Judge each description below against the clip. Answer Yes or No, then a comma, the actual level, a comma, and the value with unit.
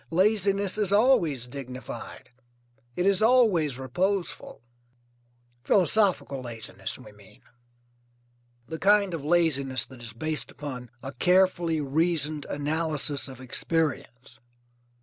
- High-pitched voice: No, medium, 155 Hz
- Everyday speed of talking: No, slow, 105 wpm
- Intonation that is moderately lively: No, wide, 6.2 semitones